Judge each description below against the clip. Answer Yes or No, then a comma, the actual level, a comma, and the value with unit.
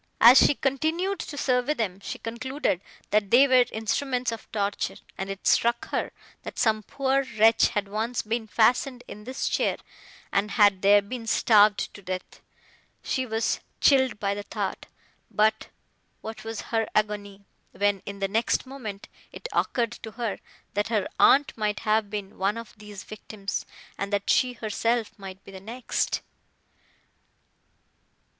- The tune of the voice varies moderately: Yes, average, 3.3 semitones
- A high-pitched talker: Yes, high, 220 Hz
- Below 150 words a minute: No, average, 155 wpm